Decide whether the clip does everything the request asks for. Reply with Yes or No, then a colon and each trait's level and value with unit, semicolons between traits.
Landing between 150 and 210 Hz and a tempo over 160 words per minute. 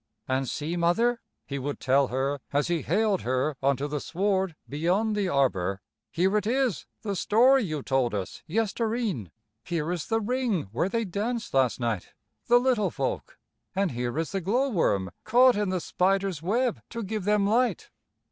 Yes: medium, 185 Hz; average, 180 wpm